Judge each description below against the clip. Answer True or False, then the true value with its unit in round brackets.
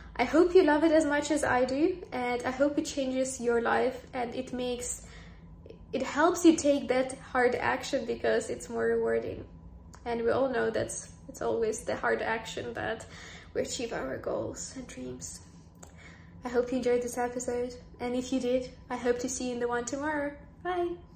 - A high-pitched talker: True (250 Hz)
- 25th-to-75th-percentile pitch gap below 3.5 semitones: True (3.1 semitones)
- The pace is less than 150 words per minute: False (195 wpm)